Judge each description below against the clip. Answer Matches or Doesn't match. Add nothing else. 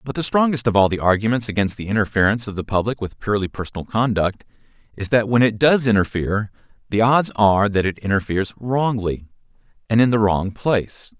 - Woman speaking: Doesn't match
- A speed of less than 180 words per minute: Doesn't match